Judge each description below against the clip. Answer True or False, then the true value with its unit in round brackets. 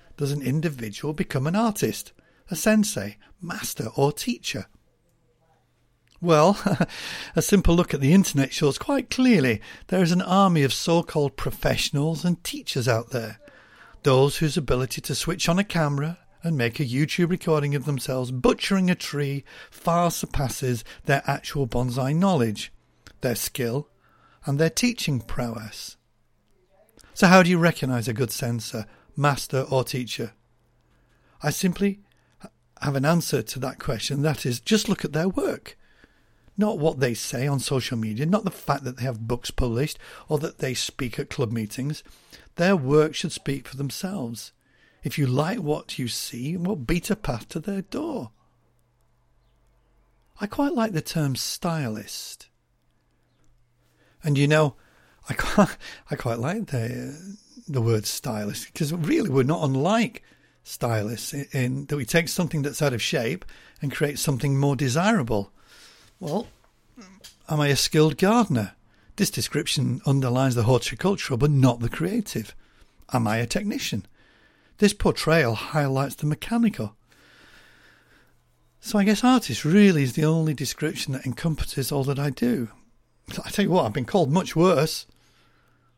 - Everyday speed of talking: True (150 wpm)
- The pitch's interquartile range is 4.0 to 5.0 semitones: False (5.5 semitones)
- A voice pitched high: False (145 Hz)